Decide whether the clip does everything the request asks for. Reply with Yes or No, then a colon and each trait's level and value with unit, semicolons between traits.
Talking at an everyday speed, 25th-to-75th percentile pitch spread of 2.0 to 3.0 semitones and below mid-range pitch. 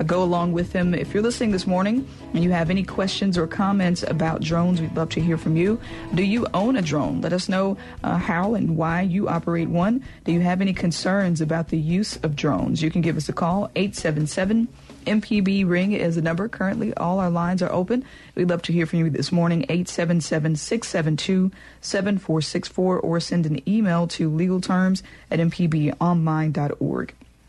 No: average, 185 wpm; average, 2.7 semitones; medium, 175 Hz